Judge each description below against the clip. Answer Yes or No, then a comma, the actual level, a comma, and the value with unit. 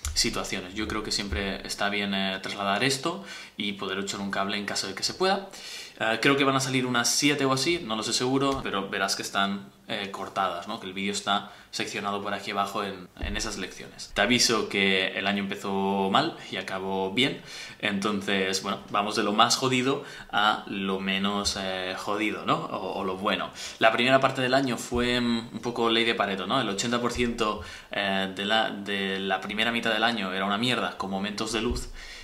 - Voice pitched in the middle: No, low, 100 Hz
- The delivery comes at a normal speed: No, fast, 205 wpm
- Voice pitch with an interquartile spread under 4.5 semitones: Yes, average, 3.5 semitones